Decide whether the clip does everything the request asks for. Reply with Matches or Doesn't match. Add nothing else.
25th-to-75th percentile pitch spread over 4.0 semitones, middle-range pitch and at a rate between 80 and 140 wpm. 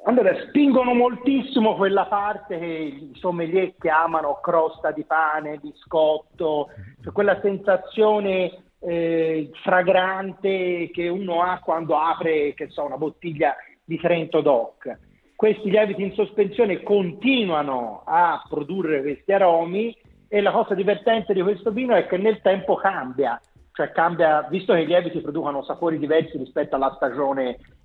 Matches